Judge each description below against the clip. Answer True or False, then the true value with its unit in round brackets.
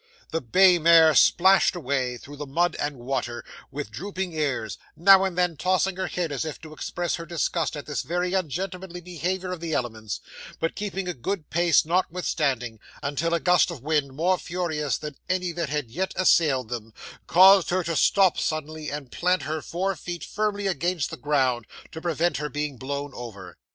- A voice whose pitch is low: False (165 Hz)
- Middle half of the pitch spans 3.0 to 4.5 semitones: True (4.1 semitones)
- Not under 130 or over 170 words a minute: False (185 wpm)